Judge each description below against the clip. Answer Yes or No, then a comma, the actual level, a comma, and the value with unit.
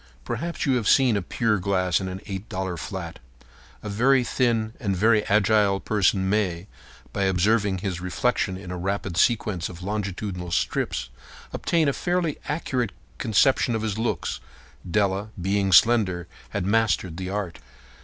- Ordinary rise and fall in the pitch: Yes, average, 3.3 semitones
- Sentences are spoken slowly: No, average, 150 wpm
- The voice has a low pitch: Yes, low, 100 Hz